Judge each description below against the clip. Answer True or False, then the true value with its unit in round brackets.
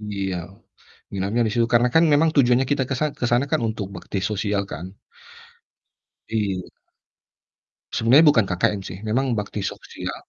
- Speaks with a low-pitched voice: True (110 Hz)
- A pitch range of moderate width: True (4.0 semitones)